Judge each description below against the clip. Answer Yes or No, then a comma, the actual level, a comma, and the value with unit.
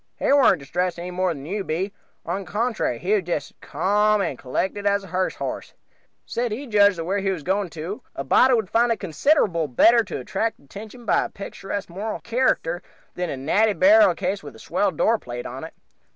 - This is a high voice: Yes, high, 195 Hz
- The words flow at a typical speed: No, fast, 210 wpm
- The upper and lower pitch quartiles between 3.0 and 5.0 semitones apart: Yes, average, 4.6 semitones